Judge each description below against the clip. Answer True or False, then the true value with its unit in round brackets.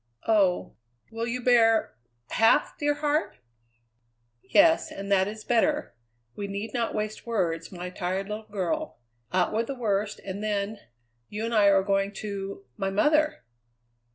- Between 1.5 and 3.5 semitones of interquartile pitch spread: True (3.1 semitones)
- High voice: True (210 Hz)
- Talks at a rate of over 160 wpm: False (150 wpm)